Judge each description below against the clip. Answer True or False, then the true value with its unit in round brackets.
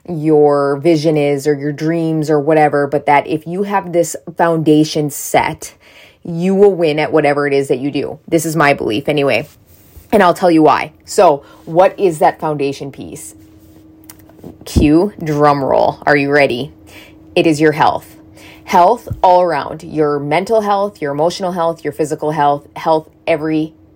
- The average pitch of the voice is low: False (155 Hz)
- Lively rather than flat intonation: False (2.6 semitones)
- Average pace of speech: True (165 wpm)